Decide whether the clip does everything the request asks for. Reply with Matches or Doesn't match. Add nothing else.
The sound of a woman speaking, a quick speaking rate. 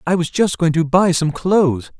Doesn't match